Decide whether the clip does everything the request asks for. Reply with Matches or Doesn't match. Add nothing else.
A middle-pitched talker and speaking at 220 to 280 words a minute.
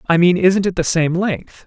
Matches